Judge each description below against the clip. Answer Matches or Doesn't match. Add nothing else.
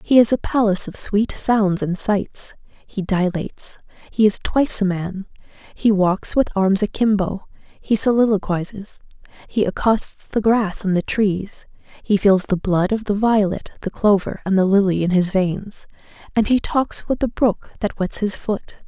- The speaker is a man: Doesn't match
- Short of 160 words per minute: Doesn't match